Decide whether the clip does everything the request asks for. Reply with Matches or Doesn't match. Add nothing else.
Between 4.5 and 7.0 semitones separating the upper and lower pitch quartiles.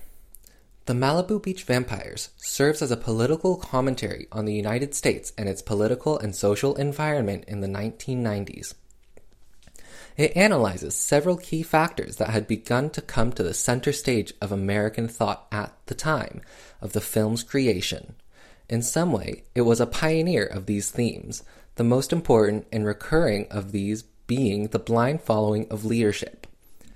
Matches